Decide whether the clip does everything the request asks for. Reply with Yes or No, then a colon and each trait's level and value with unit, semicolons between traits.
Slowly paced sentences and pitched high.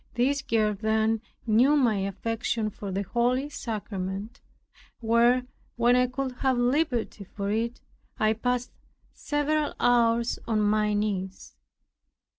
Yes: slow, 120 wpm; high, 230 Hz